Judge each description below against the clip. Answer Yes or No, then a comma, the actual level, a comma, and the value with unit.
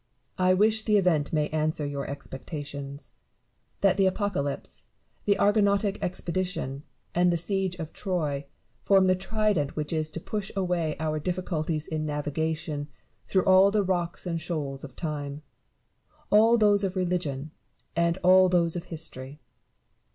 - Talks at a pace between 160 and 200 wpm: No, average, 150 wpm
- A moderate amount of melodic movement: Yes, average, 4.1 semitones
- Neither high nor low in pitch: Yes, medium, 170 Hz